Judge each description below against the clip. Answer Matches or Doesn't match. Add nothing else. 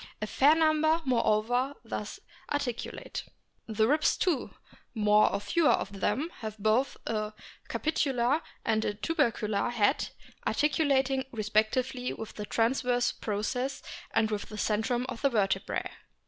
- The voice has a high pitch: Matches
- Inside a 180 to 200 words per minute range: Doesn't match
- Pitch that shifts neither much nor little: Matches